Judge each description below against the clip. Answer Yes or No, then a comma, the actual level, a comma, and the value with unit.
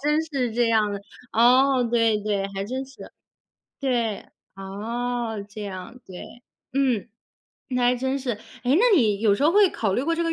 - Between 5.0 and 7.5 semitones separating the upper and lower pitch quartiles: No, average, 4.1 semitones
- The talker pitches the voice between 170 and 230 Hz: No, high, 240 Hz